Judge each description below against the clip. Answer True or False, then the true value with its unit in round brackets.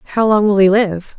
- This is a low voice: False (205 Hz)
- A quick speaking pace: True (255 wpm)